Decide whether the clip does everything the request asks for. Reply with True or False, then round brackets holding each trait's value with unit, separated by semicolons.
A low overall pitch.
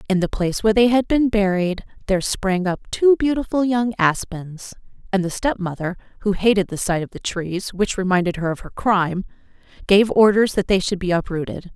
False (200 Hz)